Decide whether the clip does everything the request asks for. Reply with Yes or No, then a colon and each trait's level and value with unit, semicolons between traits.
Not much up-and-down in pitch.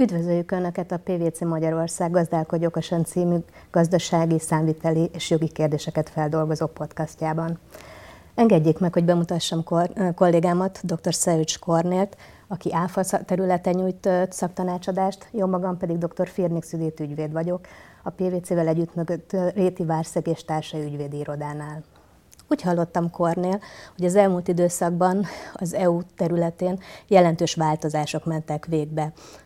Yes: narrow, 2.2 semitones